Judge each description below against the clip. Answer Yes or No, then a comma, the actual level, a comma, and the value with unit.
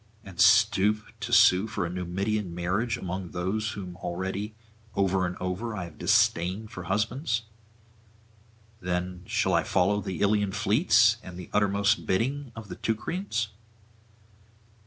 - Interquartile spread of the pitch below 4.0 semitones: Yes, average, 3.1 semitones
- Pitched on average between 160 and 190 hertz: No, low, 100 Hz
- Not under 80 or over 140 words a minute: Yes, slow, 135 wpm